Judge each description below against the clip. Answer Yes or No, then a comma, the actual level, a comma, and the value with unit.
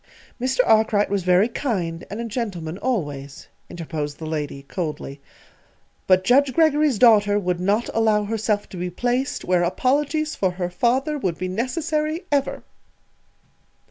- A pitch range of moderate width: No, wide, 6.4 semitones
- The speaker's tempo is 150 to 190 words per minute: No, average, 140 wpm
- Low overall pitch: No, high, 205 Hz